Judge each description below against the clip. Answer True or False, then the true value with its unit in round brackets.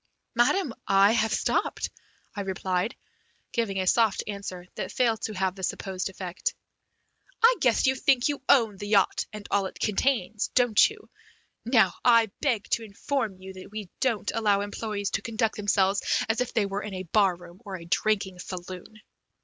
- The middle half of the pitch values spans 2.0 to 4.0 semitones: True (3.2 semitones)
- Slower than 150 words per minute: False (175 wpm)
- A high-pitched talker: True (205 Hz)